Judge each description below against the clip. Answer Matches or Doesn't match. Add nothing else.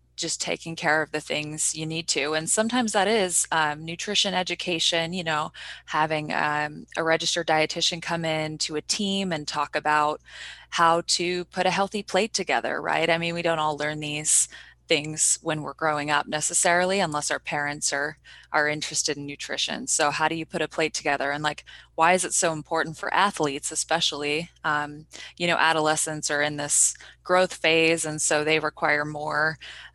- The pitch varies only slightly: Matches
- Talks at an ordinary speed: Matches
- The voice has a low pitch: Doesn't match